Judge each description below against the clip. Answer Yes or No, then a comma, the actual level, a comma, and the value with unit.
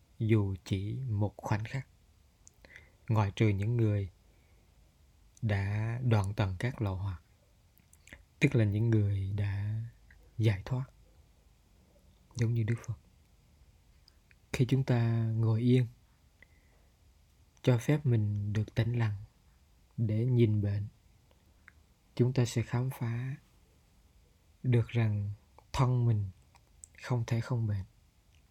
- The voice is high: No, low, 105 Hz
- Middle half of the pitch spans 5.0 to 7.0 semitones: No, average, 4.6 semitones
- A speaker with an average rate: No, slow, 110 wpm